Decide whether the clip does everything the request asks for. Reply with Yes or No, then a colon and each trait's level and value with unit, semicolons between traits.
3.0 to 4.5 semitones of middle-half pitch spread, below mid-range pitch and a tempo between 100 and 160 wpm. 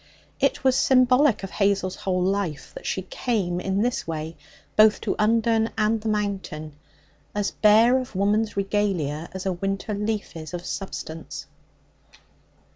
No: average, 3.3 semitones; high, 200 Hz; average, 145 wpm